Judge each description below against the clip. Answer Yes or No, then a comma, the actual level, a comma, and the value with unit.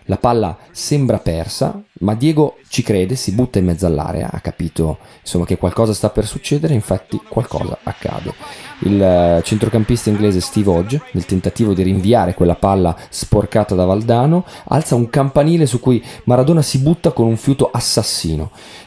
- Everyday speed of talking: Yes, average, 160 wpm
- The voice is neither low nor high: No, low, 110 Hz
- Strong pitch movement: Yes, wide, 5.9 semitones